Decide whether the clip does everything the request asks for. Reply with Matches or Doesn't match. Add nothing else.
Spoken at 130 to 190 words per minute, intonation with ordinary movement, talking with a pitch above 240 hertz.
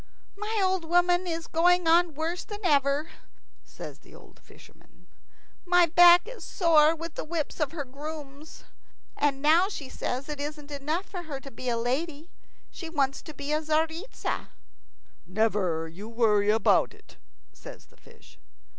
Matches